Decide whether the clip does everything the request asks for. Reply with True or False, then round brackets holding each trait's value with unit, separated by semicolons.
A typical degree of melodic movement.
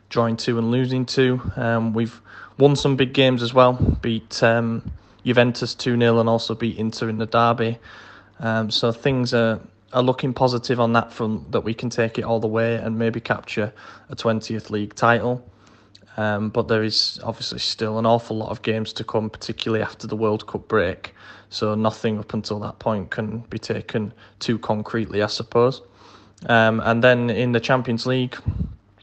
False (1.7 semitones)